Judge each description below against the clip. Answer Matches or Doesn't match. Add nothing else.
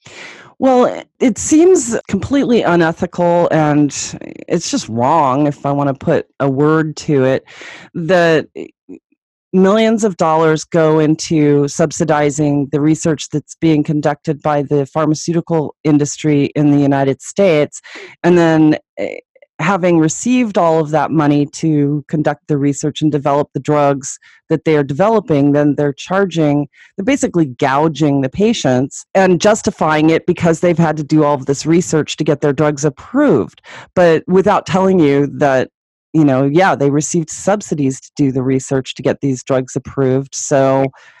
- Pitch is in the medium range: Matches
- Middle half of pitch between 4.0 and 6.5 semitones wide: Doesn't match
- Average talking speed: Matches